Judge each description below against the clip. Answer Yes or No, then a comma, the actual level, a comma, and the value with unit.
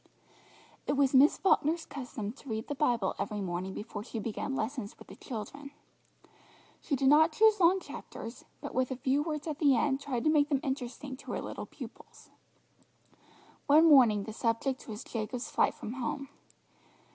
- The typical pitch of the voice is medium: No, very high, 265 Hz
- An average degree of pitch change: Yes, average, 4.2 semitones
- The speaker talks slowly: No, average, 175 wpm